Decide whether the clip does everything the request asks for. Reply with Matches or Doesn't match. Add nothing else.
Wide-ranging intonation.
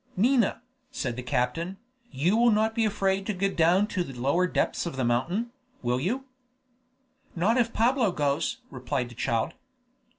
Matches